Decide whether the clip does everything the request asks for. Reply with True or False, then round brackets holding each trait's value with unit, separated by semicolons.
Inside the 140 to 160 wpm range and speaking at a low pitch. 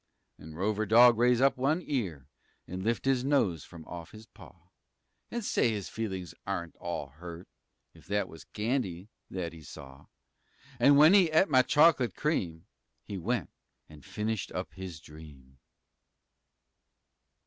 True (150 wpm; 100 Hz)